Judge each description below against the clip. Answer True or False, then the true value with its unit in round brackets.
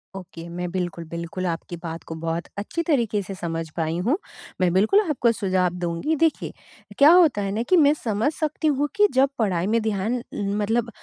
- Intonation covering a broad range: True (6.8 semitones)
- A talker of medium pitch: False (200 Hz)